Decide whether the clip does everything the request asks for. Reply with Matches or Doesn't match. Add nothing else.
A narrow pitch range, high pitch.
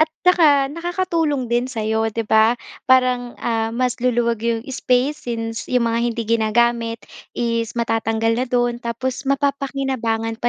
Matches